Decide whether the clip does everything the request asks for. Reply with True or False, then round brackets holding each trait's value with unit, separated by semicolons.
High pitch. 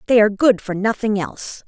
True (210 Hz)